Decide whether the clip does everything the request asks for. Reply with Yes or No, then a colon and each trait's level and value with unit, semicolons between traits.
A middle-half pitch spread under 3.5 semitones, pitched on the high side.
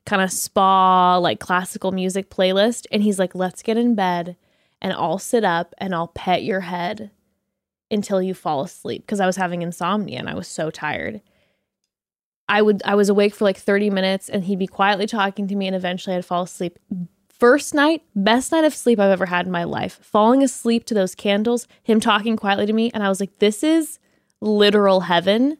Yes: narrow, 2.5 semitones; high, 200 Hz